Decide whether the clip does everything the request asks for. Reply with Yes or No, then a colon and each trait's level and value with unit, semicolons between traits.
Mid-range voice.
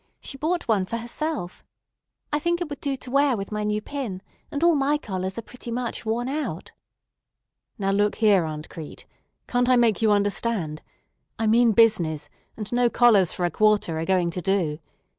No: high, 220 Hz